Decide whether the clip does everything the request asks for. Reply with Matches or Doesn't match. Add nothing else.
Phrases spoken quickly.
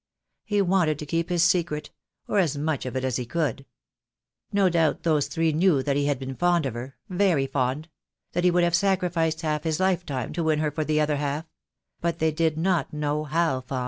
Matches